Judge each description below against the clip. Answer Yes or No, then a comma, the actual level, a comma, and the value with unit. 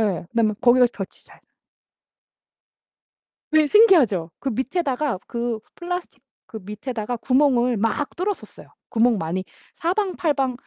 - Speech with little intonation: No, wide, 5.6 semitones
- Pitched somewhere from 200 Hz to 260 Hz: Yes, very high, 250 Hz